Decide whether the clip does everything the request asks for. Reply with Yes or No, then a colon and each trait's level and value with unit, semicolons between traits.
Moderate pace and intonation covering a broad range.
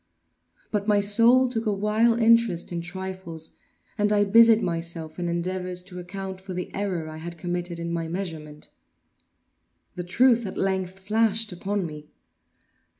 No: average, 150 wpm; average, 3.5 semitones